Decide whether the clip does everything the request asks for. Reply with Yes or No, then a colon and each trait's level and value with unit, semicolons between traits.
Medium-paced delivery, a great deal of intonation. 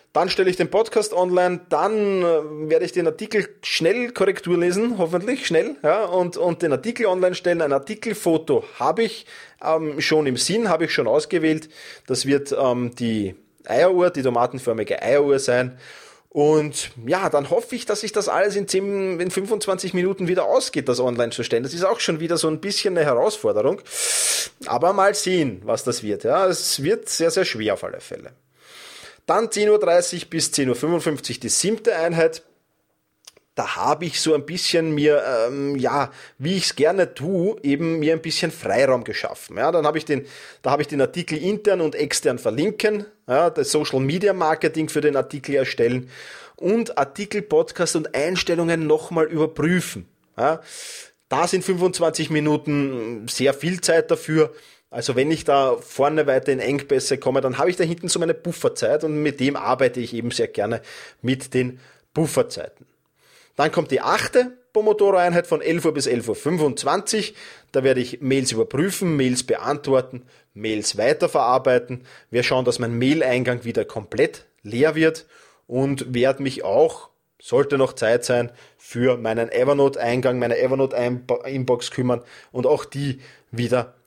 Yes: average, 165 wpm; wide, 6.2 semitones